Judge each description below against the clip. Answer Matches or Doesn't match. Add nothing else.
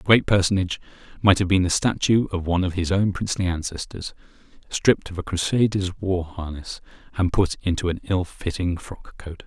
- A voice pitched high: Doesn't match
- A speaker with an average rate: Matches